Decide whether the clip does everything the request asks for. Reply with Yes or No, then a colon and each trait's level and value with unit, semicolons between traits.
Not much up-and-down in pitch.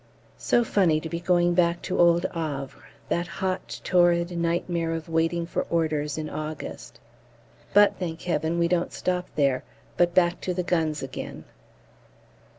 Yes: narrow, 1.6 semitones